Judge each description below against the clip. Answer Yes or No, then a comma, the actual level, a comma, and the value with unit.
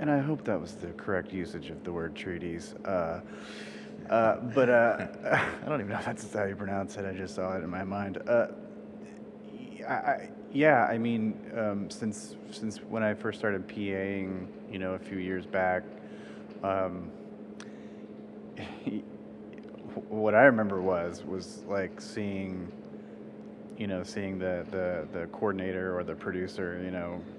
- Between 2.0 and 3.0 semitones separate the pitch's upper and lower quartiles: Yes, narrow, 2.4 semitones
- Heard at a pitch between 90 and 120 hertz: Yes, very low, 95 Hz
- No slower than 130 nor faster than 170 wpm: Yes, average, 160 wpm